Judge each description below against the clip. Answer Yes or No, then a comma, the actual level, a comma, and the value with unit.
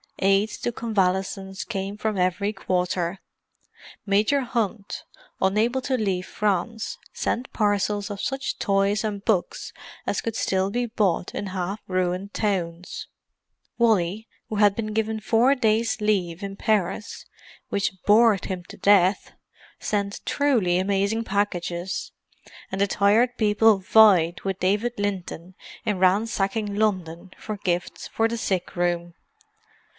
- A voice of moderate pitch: No, high, 200 Hz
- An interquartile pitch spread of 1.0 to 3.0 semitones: Yes, average, 2.7 semitones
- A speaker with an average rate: No, slow, 125 wpm